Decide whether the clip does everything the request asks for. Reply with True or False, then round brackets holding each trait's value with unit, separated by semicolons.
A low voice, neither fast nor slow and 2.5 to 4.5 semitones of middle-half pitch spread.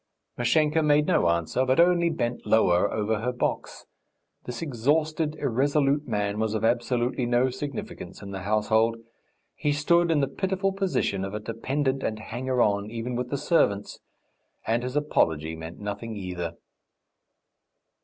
False (120 Hz; 150 wpm; 5.6 semitones)